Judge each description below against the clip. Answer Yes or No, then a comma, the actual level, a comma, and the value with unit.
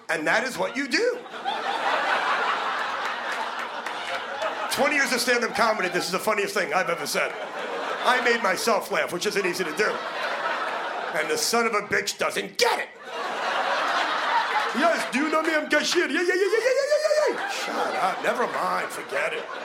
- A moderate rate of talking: Yes, average, 175 wpm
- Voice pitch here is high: Yes, very high, 300 Hz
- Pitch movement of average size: No, wide, 7.9 semitones